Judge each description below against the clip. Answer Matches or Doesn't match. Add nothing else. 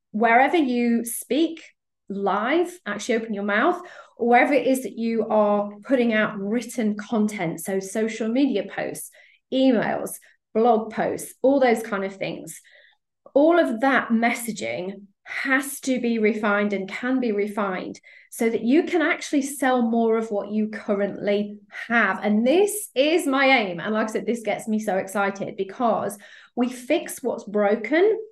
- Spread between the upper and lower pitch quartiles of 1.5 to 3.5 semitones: Doesn't match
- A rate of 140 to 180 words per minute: Matches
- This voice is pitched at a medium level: Doesn't match